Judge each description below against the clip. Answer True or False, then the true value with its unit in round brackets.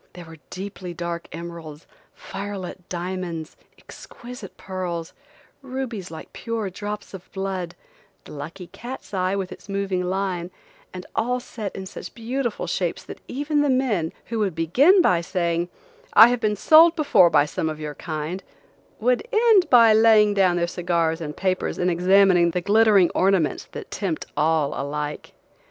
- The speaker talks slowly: False (160 wpm)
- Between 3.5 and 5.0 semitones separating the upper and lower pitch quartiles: True (4.4 semitones)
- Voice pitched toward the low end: False (185 Hz)